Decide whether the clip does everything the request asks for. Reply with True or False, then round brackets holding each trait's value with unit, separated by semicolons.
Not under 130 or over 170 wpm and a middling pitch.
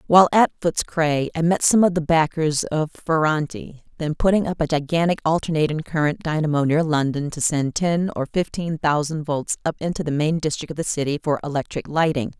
False (195 wpm; 155 Hz)